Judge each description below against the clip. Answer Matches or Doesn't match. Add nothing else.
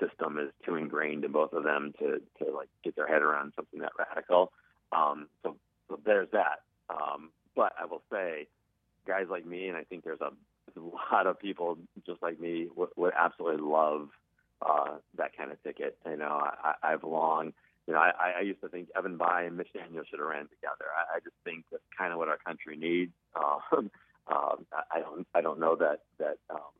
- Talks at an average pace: Doesn't match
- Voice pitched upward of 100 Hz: Doesn't match